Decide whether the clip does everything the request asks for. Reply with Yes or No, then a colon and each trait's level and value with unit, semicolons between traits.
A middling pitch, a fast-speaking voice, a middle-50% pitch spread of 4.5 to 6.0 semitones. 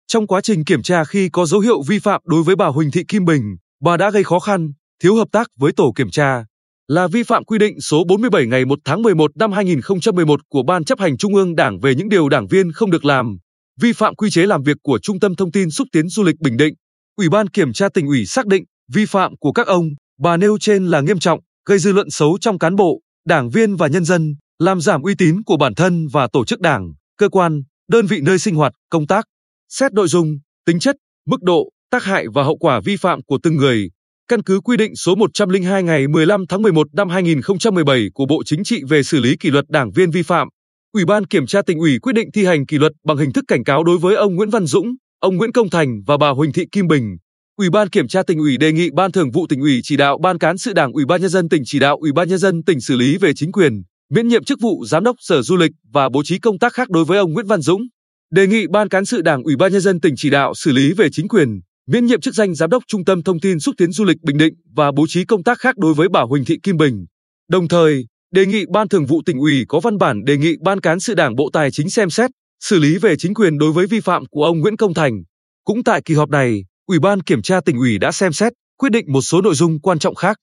Yes: medium, 175 Hz; fast, 270 wpm; average, 5.2 semitones